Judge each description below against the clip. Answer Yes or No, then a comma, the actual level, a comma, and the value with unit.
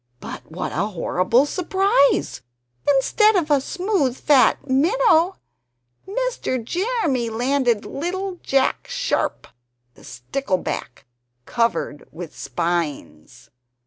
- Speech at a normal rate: No, slow, 95 wpm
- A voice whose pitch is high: Yes, very high, 270 Hz